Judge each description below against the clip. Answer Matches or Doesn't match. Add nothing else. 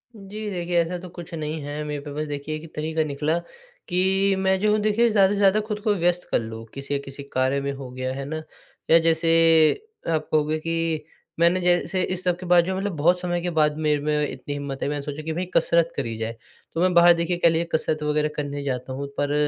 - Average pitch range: Matches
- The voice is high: Doesn't match